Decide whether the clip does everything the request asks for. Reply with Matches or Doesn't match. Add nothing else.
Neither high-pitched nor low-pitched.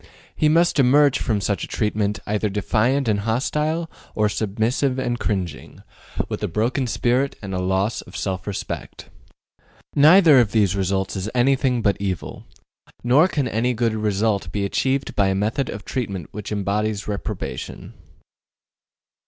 Doesn't match